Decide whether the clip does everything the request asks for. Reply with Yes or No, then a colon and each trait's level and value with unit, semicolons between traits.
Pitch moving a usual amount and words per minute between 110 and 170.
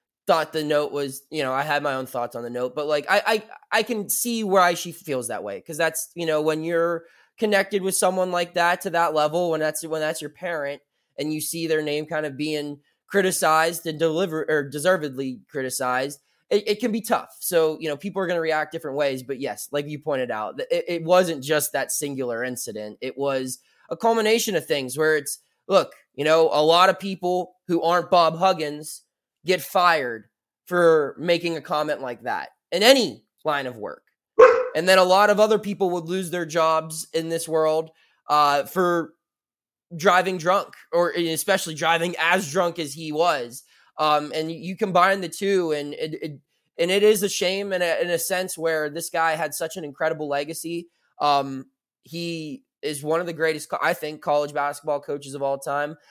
No: average, 3.4 semitones; average, 200 wpm